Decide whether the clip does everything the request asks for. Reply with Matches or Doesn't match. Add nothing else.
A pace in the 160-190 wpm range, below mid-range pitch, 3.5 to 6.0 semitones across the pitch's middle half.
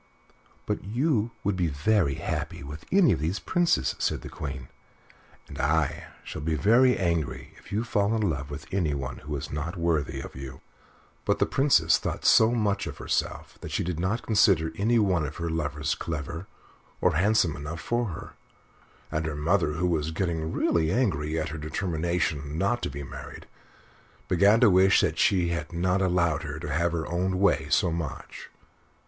Matches